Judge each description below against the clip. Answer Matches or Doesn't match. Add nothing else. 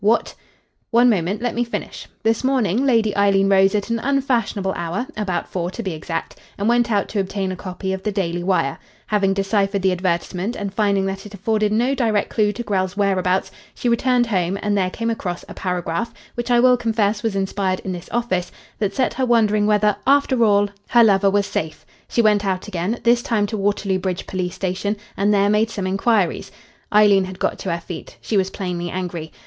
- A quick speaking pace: Matches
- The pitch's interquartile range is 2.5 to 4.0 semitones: Matches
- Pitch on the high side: Matches